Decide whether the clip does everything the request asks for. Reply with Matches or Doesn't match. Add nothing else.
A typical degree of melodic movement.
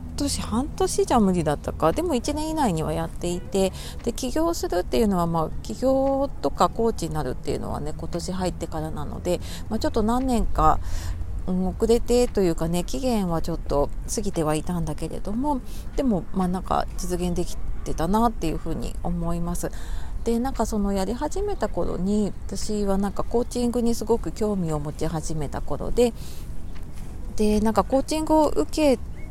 Doesn't match